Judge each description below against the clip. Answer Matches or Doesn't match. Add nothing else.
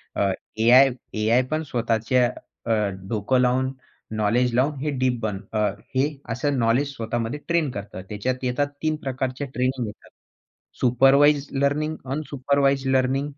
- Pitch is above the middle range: Doesn't match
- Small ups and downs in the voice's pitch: Doesn't match